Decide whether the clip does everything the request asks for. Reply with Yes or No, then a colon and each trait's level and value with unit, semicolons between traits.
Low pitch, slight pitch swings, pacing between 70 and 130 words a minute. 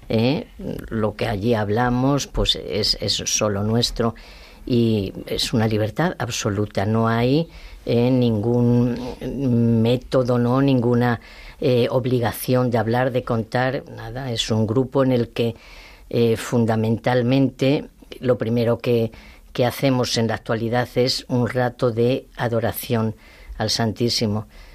Yes: low, 120 Hz; narrow, 2.0 semitones; slow, 125 wpm